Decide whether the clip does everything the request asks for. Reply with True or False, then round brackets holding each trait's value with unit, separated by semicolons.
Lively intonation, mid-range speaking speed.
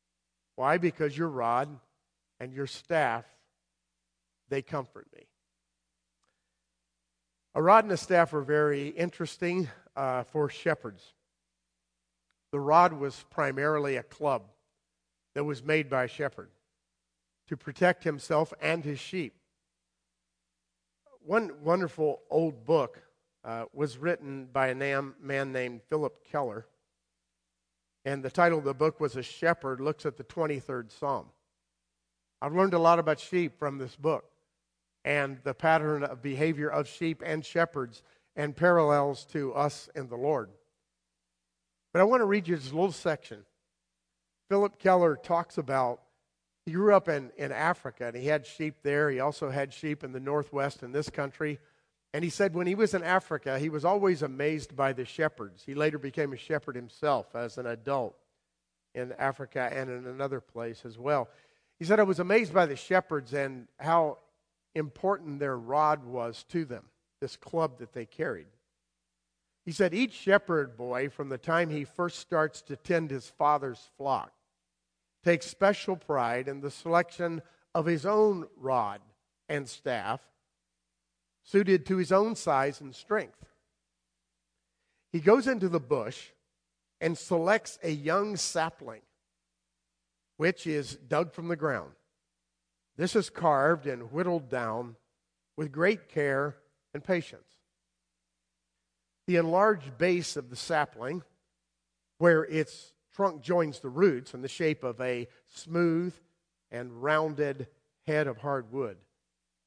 True (6.7 semitones; 145 wpm)